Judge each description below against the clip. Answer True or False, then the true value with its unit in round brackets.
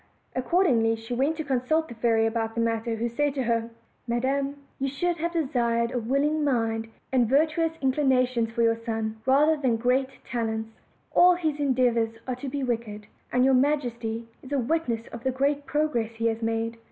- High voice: True (250 Hz)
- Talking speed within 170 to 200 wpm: True (185 wpm)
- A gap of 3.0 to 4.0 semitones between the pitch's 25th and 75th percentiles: True (3.7 semitones)